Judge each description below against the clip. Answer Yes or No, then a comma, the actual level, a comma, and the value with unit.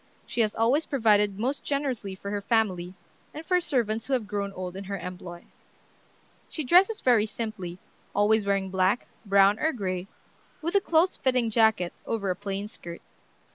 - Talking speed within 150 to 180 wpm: Yes, average, 170 wpm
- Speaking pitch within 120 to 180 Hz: No, high, 210 Hz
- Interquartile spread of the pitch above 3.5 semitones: Yes, average, 4.4 semitones